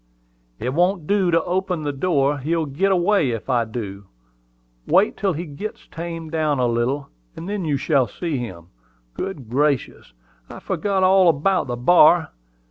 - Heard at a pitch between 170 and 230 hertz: No, medium, 155 Hz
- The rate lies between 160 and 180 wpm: Yes, average, 165 wpm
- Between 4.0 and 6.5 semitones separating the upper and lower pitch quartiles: Yes, wide, 5.5 semitones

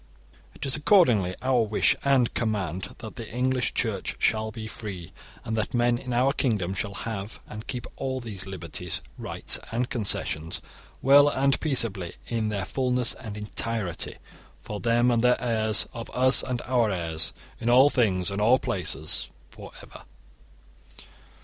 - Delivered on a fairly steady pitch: No, average, 3.9 semitones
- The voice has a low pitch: Yes, low, 115 Hz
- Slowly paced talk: No, average, 155 wpm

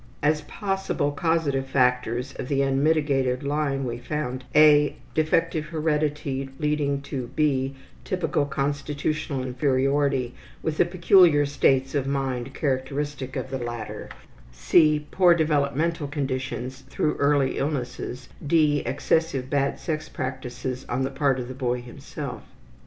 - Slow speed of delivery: Yes, slow, 125 wpm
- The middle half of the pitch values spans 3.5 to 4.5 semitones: No, narrow, 2.5 semitones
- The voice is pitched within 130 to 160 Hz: Yes, medium, 140 Hz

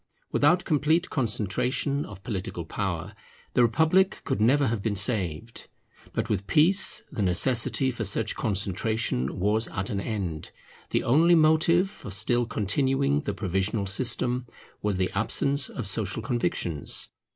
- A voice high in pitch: No, low, 115 Hz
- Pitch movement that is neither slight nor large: No, wide, 6.1 semitones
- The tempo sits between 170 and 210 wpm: No, average, 140 wpm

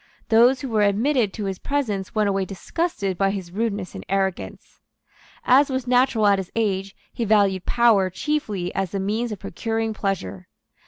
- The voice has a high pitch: Yes, high, 205 Hz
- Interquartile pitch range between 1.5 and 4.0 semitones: Yes, average, 3.5 semitones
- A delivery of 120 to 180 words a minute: Yes, average, 170 wpm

